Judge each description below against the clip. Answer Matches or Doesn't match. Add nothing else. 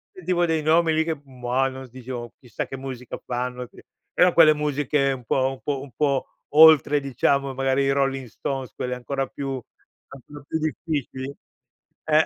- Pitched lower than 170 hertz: Matches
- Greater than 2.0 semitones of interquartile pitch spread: Matches